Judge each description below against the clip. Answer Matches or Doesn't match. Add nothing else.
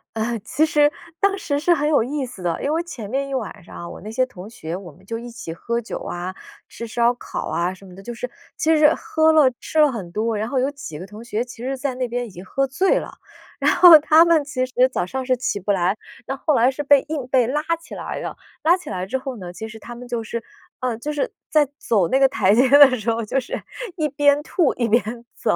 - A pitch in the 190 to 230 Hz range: Doesn't match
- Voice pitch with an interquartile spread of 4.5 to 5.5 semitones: Matches